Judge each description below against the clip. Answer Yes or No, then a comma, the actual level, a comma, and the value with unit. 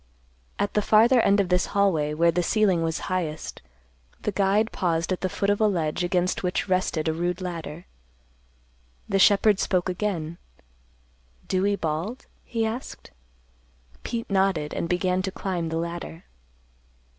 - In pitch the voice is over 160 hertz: Yes, medium, 185 Hz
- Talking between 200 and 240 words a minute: No, average, 150 wpm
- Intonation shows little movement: No, average, 3.1 semitones